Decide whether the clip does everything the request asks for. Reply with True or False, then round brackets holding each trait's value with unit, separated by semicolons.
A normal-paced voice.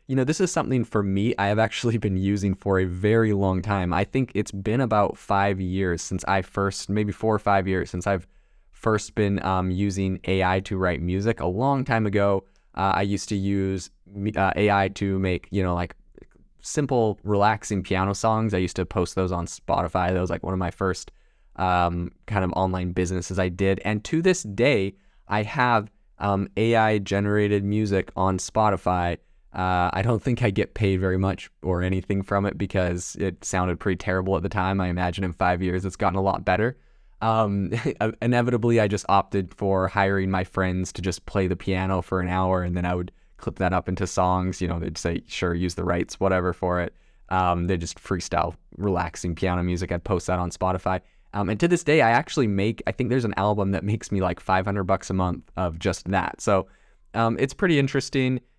False (210 wpm)